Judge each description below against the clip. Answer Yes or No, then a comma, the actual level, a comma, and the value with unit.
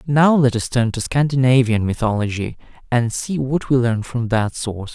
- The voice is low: Yes, low, 125 Hz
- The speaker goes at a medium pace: Yes, average, 180 wpm